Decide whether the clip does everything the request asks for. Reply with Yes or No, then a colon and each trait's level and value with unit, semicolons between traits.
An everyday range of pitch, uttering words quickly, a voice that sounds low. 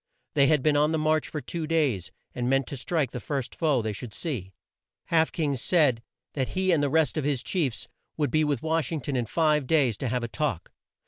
No: average, 3.9 semitones; fast, 235 wpm; medium, 145 Hz